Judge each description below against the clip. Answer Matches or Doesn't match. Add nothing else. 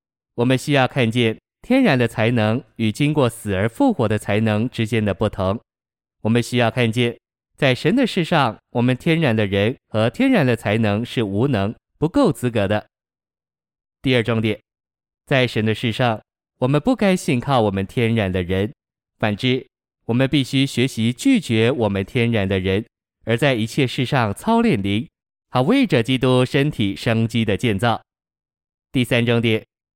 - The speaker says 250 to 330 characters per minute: Doesn't match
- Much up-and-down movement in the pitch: Doesn't match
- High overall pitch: Doesn't match